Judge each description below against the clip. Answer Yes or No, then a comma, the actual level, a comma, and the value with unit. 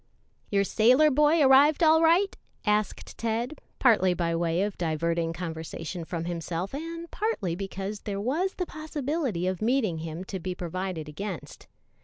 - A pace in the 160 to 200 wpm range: No, average, 150 wpm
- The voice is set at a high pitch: Yes, high, 200 Hz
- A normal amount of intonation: No, wide, 8.8 semitones